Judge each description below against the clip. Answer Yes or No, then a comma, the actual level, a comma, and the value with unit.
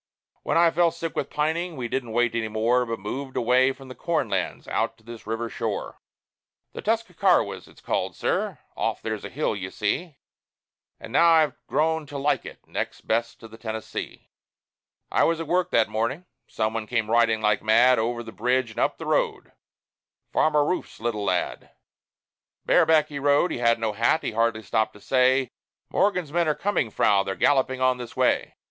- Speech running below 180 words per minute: No, average, 190 wpm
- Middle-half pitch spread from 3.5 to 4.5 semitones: No, average, 5.3 semitones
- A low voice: Yes, low, 125 Hz